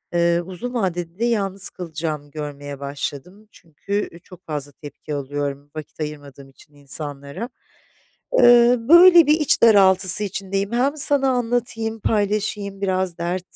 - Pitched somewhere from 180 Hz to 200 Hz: Yes, medium, 185 Hz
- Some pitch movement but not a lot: No, wide, 7.0 semitones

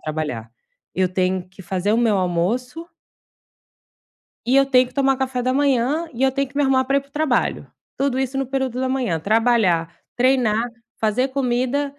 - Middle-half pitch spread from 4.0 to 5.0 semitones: Yes, average, 4.7 semitones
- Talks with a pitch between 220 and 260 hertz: Yes, very high, 250 Hz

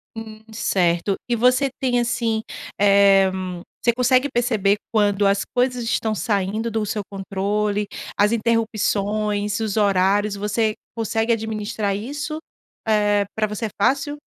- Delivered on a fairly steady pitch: Yes, narrow, 2.3 semitones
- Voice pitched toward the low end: No, high, 215 Hz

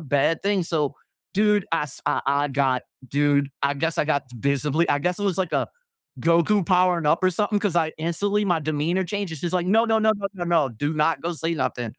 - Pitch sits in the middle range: Yes, medium, 165 Hz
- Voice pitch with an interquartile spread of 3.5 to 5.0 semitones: Yes, average, 4.2 semitones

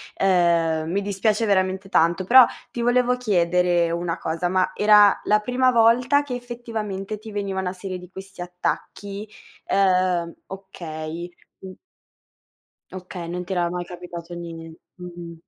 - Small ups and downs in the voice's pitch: No, average, 3.2 semitones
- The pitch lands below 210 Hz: Yes, medium, 185 Hz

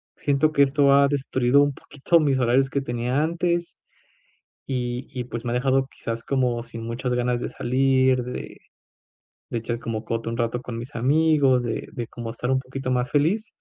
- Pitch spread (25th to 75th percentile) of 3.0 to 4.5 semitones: No, narrow, 2.5 semitones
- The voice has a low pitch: Yes, low, 130 Hz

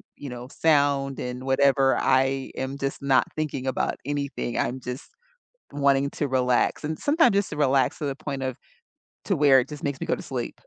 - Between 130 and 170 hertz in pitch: Yes, low, 135 Hz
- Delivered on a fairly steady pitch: Yes, narrow, 1.6 semitones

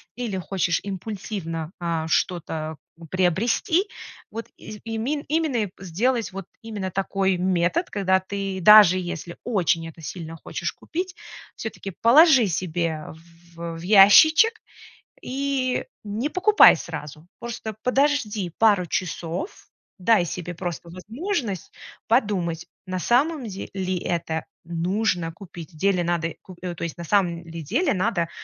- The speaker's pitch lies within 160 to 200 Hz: Yes, high, 190 Hz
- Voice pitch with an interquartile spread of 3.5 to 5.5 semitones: Yes, average, 5.0 semitones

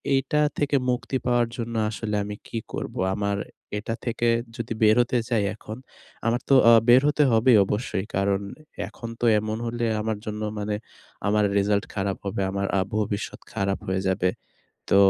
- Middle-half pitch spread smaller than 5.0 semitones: Yes, average, 2.9 semitones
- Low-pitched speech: Yes, low, 110 Hz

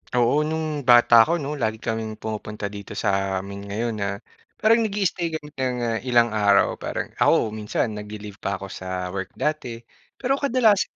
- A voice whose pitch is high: No, low, 115 Hz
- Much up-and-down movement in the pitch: Yes, wide, 6.6 semitones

